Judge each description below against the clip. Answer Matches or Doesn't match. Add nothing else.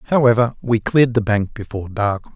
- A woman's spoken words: Doesn't match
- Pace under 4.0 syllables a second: Doesn't match